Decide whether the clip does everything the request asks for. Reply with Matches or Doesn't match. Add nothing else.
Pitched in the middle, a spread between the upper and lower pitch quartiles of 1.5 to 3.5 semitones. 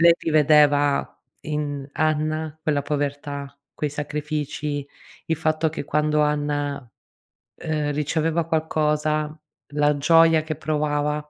Doesn't match